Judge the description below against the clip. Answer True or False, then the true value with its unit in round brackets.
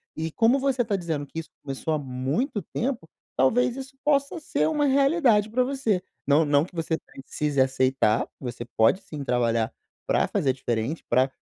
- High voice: False (160 Hz)